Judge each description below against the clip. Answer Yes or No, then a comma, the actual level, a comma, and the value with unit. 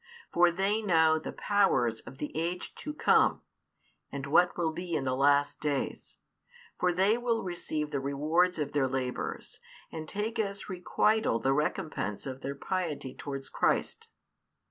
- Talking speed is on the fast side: No, average, 155 wpm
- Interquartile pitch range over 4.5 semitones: Yes, average, 5.0 semitones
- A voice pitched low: No, medium, 160 Hz